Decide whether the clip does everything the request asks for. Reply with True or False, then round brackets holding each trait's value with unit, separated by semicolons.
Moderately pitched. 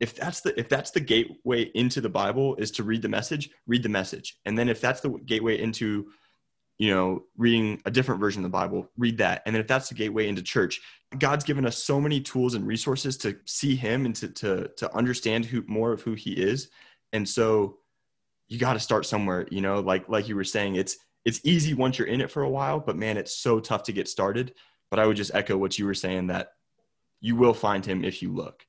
False (110 Hz)